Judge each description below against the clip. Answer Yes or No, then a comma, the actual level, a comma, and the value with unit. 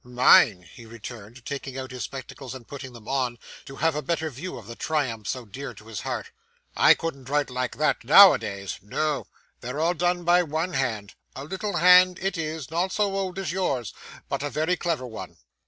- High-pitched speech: No, medium, 140 Hz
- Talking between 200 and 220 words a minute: Yes, fast, 205 wpm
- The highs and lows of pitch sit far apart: Yes, wide, 5.7 semitones